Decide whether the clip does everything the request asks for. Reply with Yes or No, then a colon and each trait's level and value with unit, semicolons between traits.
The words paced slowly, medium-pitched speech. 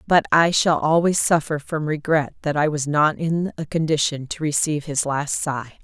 No: average, 195 wpm; medium, 155 Hz